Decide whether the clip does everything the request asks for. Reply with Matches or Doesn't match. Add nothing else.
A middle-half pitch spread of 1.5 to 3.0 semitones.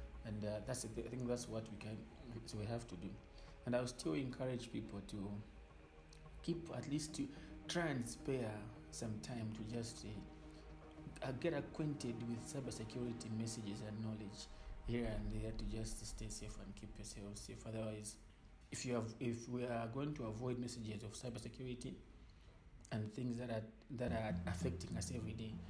Matches